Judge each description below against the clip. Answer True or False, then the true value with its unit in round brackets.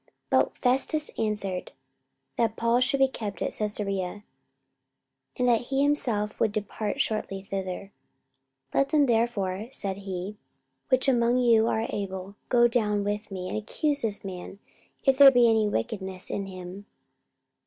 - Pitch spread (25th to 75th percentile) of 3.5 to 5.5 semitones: True (3.8 semitones)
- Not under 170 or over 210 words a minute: False (155 wpm)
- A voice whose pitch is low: False (215 Hz)